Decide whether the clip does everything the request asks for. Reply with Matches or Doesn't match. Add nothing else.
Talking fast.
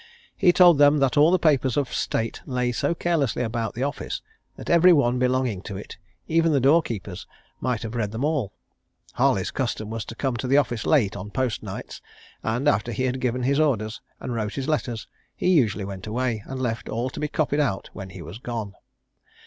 Matches